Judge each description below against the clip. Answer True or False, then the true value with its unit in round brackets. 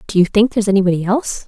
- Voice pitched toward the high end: True (205 Hz)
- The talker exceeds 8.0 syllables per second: True (8.3 syllables/s)